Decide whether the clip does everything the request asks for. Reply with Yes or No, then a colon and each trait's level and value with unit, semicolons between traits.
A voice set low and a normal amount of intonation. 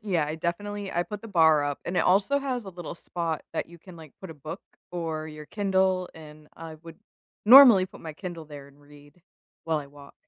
No: medium, 170 Hz; average, 3.8 semitones